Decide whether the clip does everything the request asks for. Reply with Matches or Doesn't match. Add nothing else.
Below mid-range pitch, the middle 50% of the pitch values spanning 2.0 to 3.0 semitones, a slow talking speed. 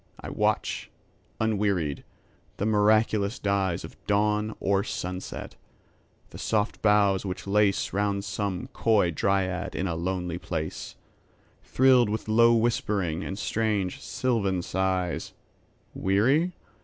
Matches